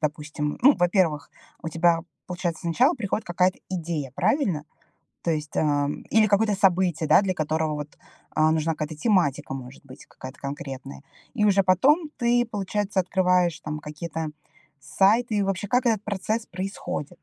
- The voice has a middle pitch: Yes, medium, 175 Hz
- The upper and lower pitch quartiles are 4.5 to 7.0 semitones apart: Yes, average, 5.0 semitones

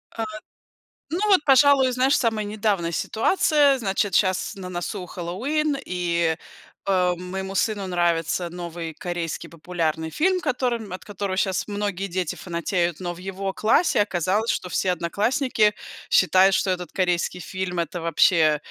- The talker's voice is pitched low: No, high, 190 Hz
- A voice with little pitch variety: No, average, 3.8 semitones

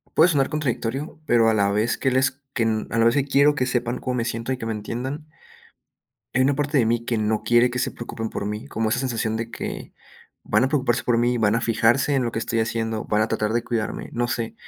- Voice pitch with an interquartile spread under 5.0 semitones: Yes, narrow, 2.6 semitones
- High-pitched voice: No, low, 120 Hz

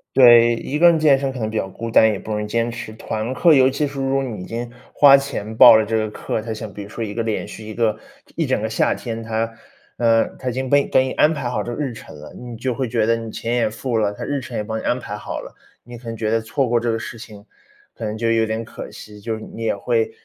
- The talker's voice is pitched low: Yes, low, 115 Hz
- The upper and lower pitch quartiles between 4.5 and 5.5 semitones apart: No, average, 2.8 semitones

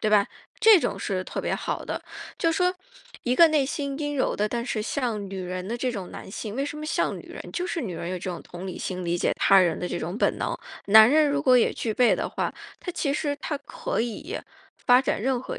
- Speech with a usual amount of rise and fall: No, wide, 6.9 semitones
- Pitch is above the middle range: Yes, high, 245 Hz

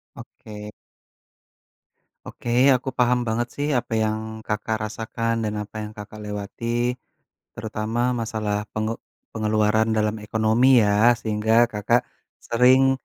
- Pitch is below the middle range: Yes, low, 110 Hz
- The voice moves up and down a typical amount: No, narrow, 1.9 semitones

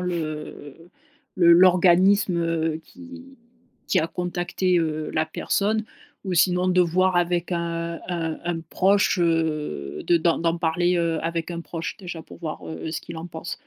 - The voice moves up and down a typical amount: No, narrow, 1.7 semitones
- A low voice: No, medium, 170 Hz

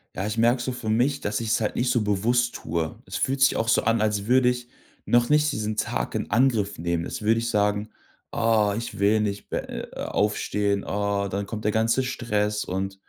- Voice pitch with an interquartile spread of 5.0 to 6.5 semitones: No, average, 2.8 semitones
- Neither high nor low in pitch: No, low, 110 Hz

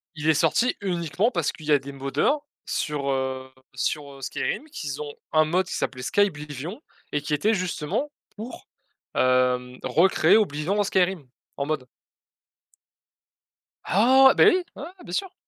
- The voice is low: No, medium, 155 Hz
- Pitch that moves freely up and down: Yes, wide, 6.5 semitones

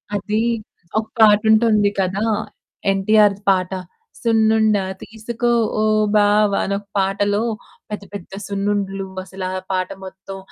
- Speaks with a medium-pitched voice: No, high, 205 Hz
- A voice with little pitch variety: Yes, narrow, 1.8 semitones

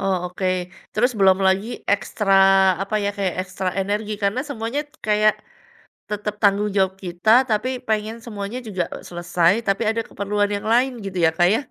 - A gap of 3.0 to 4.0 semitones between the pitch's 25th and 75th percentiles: No, narrow, 2.4 semitones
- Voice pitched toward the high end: Yes, high, 205 Hz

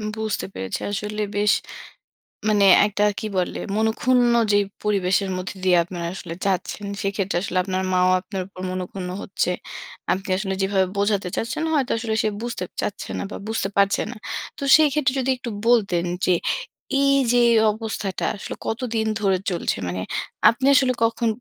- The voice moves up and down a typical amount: Yes, average, 3.2 semitones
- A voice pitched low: No, high, 205 Hz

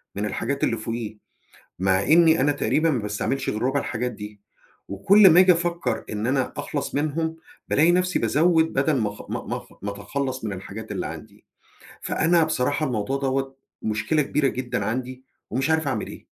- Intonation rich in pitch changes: Yes, wide, 6.3 semitones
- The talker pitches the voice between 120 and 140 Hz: Yes, low, 135 Hz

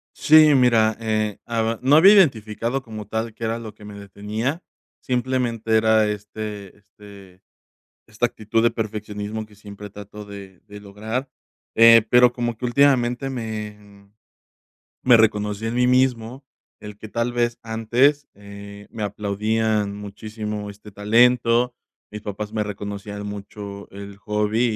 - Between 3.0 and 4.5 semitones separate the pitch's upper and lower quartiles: No, narrow, 2.4 semitones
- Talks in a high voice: No, low, 110 Hz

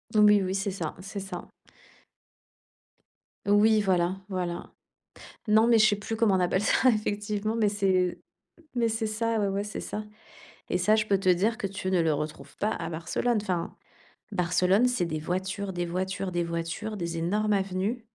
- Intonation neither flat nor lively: Yes, average, 3.0 semitones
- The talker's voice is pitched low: No, high, 195 Hz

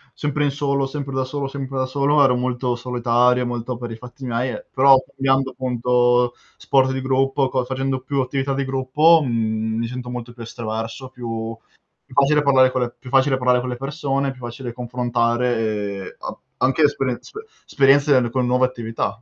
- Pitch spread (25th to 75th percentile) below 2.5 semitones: Yes, narrow, 2.0 semitones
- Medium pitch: No, low, 130 Hz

